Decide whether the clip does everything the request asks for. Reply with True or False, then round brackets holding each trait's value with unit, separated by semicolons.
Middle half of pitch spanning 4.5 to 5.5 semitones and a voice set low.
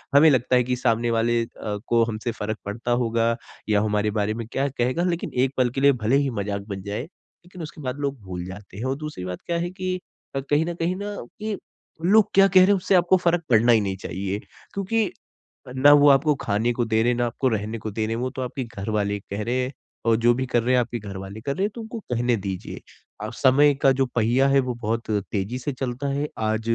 True (5.0 semitones; 120 Hz)